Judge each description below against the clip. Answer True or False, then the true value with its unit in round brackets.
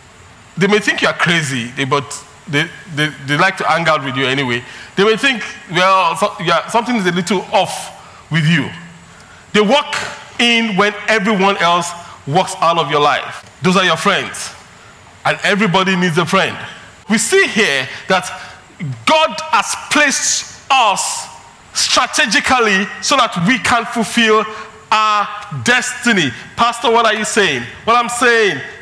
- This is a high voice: True (200 Hz)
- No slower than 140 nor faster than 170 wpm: True (155 wpm)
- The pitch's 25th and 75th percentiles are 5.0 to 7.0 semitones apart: True (5.6 semitones)